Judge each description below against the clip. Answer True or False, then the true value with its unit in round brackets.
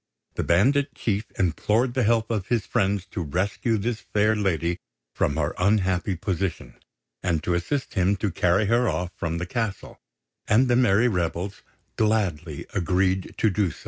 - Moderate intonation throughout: True (4.0 semitones)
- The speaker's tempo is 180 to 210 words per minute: False (165 wpm)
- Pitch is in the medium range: False (100 Hz)